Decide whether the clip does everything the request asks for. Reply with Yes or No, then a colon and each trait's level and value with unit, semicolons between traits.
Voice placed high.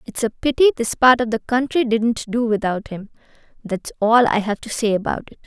Yes: high, 230 Hz